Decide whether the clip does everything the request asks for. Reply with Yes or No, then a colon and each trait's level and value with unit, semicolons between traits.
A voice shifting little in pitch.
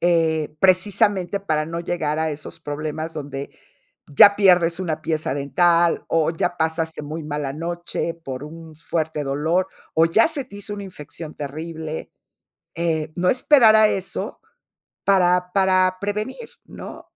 No: average, 3.2 semitones